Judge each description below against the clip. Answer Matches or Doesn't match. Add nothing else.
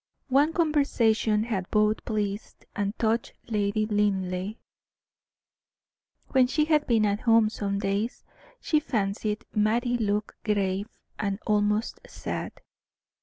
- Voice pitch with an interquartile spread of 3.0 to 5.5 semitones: Doesn't match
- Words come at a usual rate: Doesn't match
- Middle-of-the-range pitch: Doesn't match